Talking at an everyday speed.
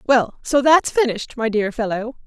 Yes: average, 185 wpm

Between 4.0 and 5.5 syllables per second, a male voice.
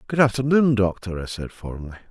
No: 6.0 syllables/s; male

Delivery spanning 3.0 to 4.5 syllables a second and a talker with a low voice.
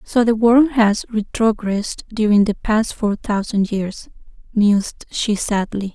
No: 4.1 syllables/s; high, 215 Hz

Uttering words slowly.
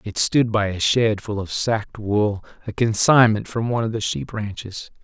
No: fast, 205 wpm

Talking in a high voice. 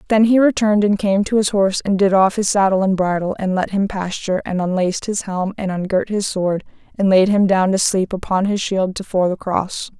Yes: high, 195 Hz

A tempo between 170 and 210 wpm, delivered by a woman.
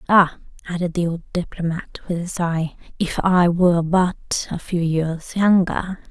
No: average, 155 wpm; female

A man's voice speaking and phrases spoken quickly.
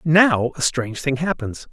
No: male; average, 175 wpm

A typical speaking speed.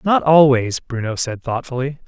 Yes: average, 145 wpm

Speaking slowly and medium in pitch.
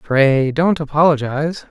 Yes: slow, 105 wpm; medium, 150 Hz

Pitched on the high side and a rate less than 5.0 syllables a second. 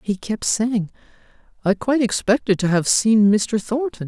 Yes: high, 215 Hz; 4.6 syllables/s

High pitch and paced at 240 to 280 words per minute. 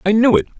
No: high, 200 Hz; fast, 300 wpm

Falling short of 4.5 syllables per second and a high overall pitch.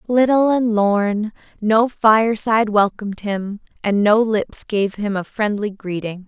Yes: 4.1 syllables/s; high, 210 Hz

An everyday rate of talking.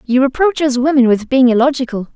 Yes: average, 195 wpm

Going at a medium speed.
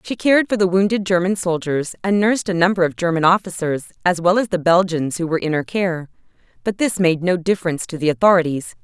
No: fast, 215 wpm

